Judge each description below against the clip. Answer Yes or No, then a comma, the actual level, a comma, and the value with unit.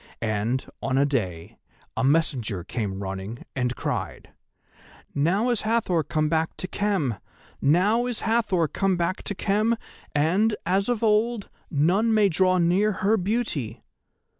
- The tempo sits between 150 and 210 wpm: No, average, 140 wpm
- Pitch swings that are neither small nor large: No, wide, 7.4 semitones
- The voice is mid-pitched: Yes, medium, 180 Hz